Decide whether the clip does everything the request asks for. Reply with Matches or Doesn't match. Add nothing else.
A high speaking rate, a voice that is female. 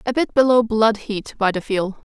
Matches